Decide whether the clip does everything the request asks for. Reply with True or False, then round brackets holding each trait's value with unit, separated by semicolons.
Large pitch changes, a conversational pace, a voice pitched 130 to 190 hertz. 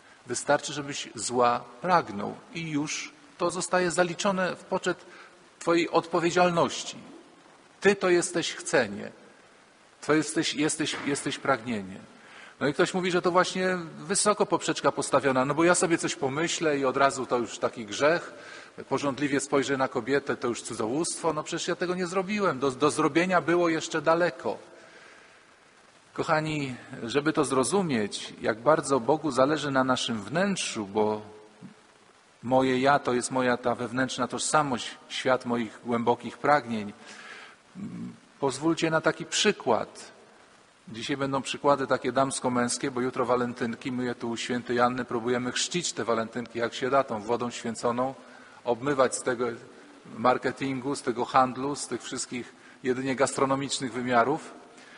False (5.0 semitones; 140 wpm; 140 Hz)